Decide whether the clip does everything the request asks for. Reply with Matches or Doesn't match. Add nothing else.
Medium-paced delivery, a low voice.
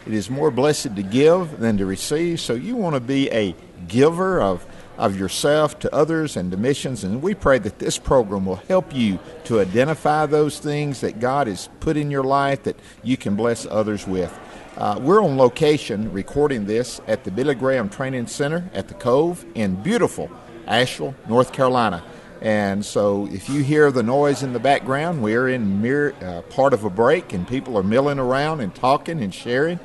Matches